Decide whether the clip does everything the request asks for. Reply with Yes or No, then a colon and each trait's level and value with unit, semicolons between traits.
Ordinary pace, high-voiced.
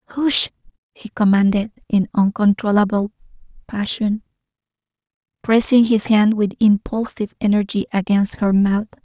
No: slow, 100 wpm; high, 210 Hz